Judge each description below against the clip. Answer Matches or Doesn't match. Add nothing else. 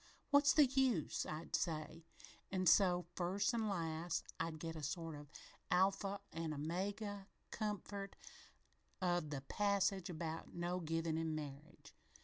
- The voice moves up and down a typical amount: Matches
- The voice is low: Doesn't match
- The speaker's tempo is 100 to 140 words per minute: Matches